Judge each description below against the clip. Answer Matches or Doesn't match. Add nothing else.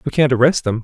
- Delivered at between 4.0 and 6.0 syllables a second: Doesn't match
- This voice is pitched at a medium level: Doesn't match